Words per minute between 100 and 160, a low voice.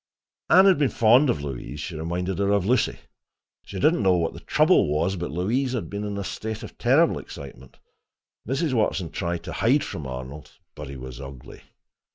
No: average, 195 wpm; very low, 95 Hz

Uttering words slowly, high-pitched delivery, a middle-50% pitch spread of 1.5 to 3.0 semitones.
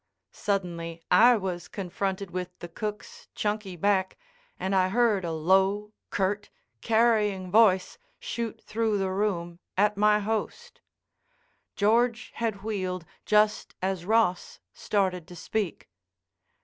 Yes: slow, 120 wpm; high, 200 Hz; narrow, 2.6 semitones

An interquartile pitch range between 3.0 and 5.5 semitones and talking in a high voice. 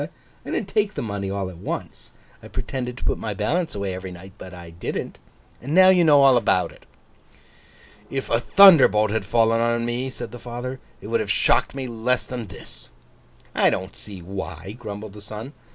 No: average, 4.6 semitones; low, 115 Hz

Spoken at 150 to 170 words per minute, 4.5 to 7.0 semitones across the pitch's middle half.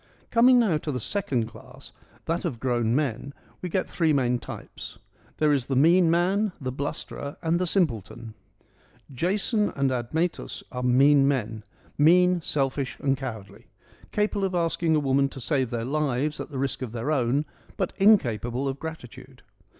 Yes: average, 165 wpm; average, 5.3 semitones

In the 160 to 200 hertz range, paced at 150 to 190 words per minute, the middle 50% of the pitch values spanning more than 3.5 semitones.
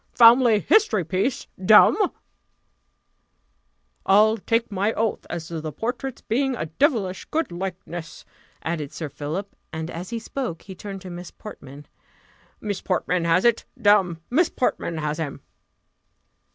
No: high, 190 Hz; average, 140 wpm; wide, 5.5 semitones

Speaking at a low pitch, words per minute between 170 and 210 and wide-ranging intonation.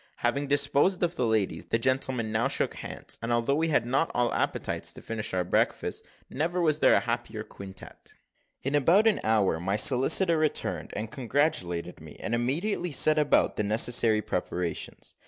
Yes: low, 125 Hz; average, 175 wpm; wide, 5.7 semitones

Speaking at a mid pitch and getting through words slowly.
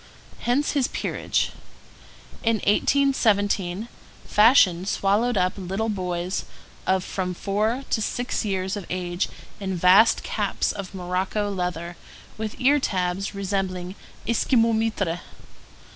No: high, 195 Hz; slow, 115 wpm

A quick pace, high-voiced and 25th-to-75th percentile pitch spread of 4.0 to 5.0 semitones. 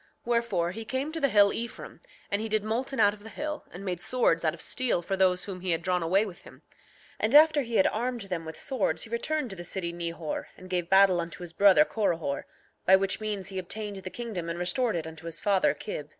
Yes: fast, 245 wpm; high, 195 Hz; average, 4.5 semitones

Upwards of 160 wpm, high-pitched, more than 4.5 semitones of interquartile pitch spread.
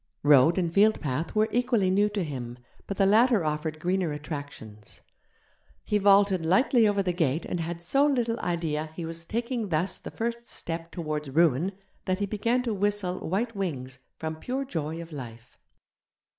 No: average, 170 wpm; medium, 180 Hz; average, 5.1 semitones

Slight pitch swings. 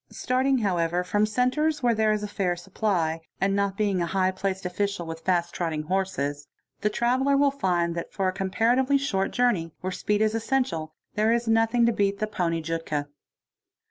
No: average, 4.7 semitones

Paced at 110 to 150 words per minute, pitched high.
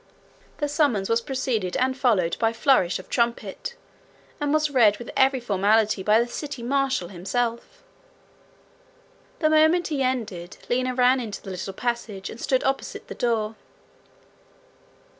Yes: average, 140 wpm; high, 240 Hz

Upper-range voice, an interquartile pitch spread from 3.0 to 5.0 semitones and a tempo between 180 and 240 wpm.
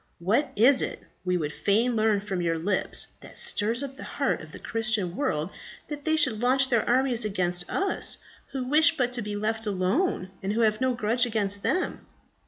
Yes: high, 225 Hz; average, 4.4 semitones; average, 195 wpm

